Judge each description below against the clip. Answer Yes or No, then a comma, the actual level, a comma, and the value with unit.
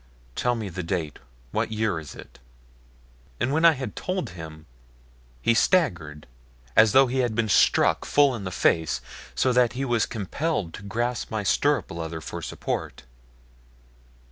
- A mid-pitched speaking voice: No, low, 110 Hz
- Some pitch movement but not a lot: No, wide, 6.9 semitones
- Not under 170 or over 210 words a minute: No, average, 160 wpm